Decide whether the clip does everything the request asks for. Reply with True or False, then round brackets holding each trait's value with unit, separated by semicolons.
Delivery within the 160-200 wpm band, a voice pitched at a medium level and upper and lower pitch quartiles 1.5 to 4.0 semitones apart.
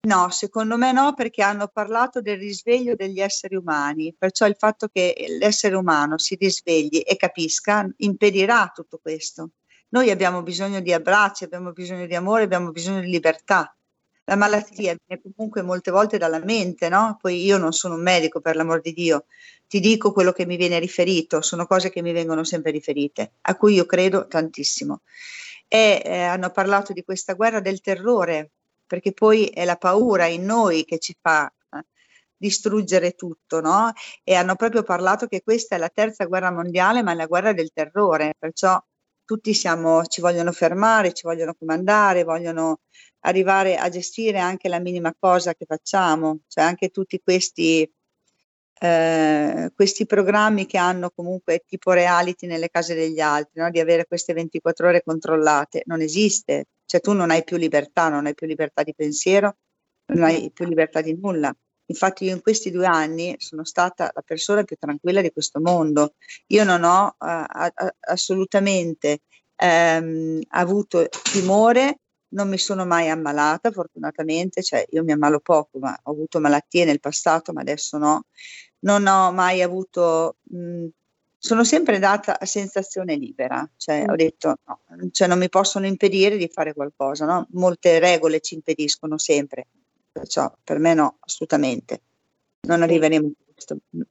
True (165 wpm; 180 Hz; 3.5 semitones)